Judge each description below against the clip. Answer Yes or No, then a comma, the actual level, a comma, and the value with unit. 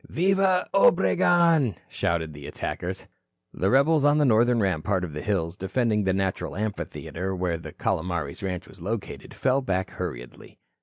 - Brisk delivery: No, average, 145 wpm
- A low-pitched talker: Yes, very low, 95 Hz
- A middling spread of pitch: No, wide, 7.2 semitones